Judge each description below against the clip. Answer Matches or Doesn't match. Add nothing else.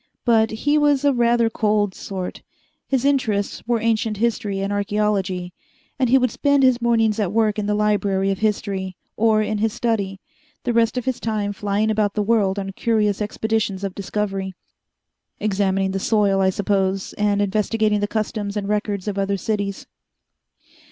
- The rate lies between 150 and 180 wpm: Matches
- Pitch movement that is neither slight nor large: Doesn't match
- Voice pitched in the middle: Doesn't match